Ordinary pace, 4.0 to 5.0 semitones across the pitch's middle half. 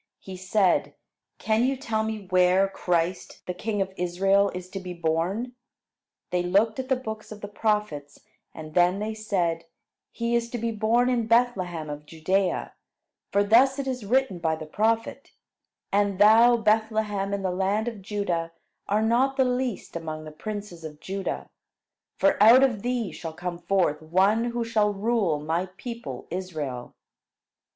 Yes: average, 165 wpm; average, 4.3 semitones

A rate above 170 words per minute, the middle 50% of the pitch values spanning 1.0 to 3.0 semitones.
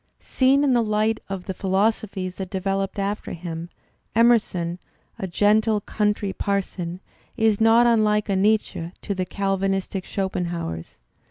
No: average, 140 wpm; average, 2.7 semitones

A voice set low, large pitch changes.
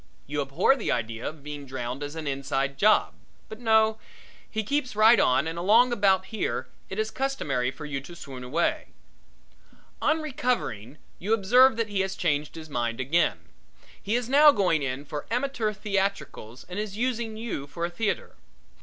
No: high, 190 Hz; wide, 7.8 semitones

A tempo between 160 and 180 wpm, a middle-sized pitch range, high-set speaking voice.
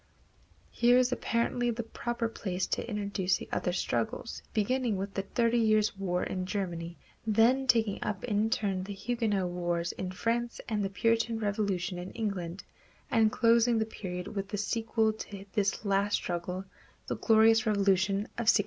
Yes: average, 165 wpm; average, 3.1 semitones; high, 210 Hz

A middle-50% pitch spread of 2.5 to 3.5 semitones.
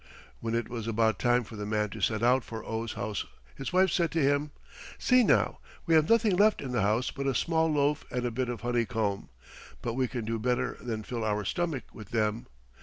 No: average, 4.4 semitones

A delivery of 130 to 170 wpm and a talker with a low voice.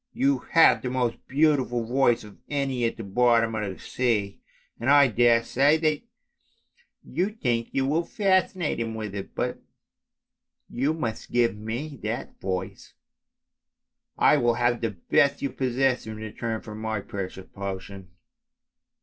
Yes: average, 145 wpm; low, 120 Hz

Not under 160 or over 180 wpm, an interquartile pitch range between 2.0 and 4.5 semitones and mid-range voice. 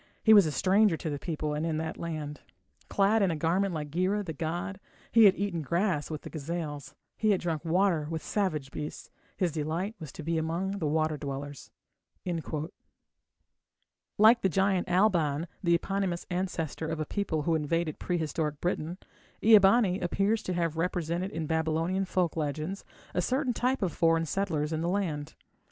Yes: average, 175 wpm; average, 3.7 semitones; medium, 170 Hz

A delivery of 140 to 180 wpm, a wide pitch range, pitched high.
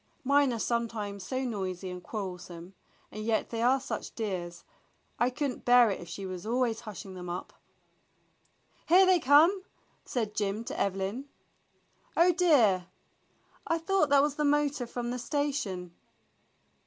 Yes: average, 155 wpm; wide, 6.5 semitones; high, 235 Hz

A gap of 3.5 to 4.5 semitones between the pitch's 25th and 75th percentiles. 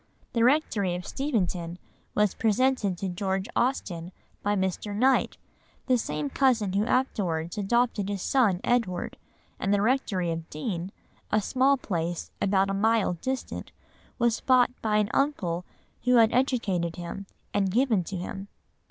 No: average, 5.2 semitones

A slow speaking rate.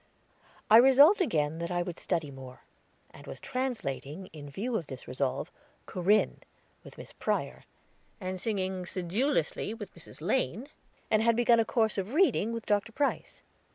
No: average, 155 wpm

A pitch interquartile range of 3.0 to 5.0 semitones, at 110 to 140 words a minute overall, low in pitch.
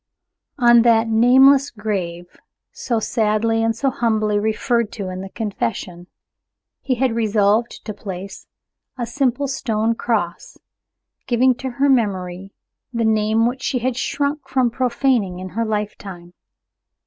No: average, 3.4 semitones; slow, 135 wpm; high, 225 Hz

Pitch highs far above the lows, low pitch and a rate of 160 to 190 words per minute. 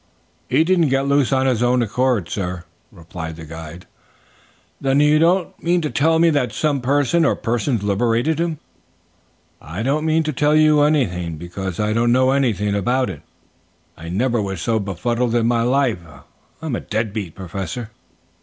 Yes: wide, 6.7 semitones; low, 120 Hz; average, 170 wpm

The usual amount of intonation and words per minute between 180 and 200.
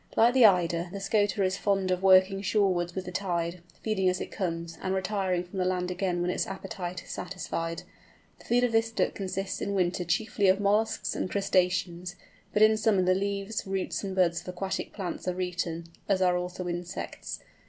No: narrow, 1.8 semitones; average, 195 wpm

